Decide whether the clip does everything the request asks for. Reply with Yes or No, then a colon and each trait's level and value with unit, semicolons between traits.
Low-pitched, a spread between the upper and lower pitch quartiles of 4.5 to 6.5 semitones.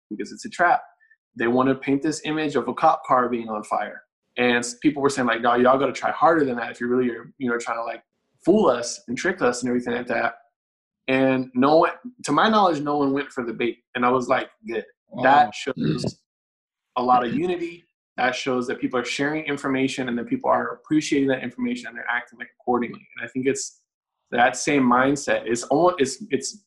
No: low, 130 Hz; average, 3.0 semitones